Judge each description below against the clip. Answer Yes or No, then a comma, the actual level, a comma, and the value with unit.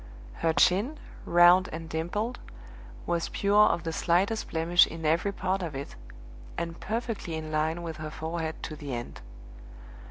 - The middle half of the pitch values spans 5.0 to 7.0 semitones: No, average, 2.8 semitones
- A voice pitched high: No, medium, 170 Hz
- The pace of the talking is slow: No, average, 155 wpm